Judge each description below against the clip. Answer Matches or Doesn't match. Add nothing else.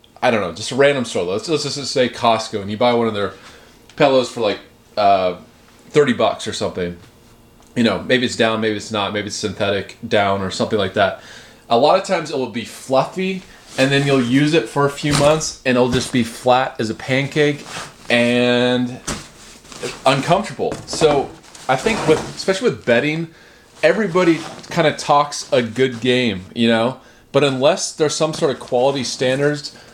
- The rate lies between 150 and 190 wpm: Matches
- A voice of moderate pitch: Doesn't match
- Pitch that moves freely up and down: Doesn't match